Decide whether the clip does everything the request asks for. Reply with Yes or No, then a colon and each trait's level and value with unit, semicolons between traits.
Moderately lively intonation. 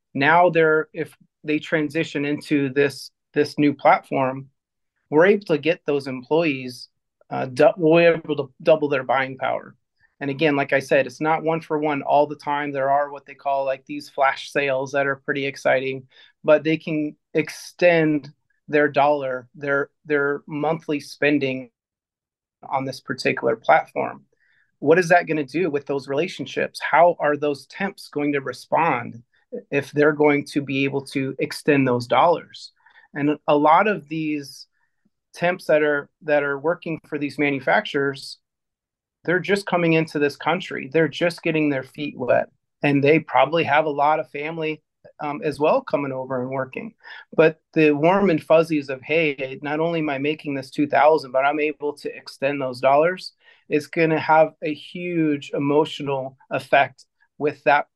No: narrow, 2.2 semitones